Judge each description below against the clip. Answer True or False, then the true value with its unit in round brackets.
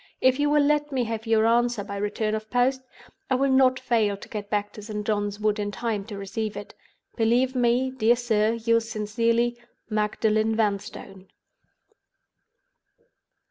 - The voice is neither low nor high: False (225 Hz)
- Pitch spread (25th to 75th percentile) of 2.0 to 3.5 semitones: True (2.7 semitones)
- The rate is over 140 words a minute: True (160 wpm)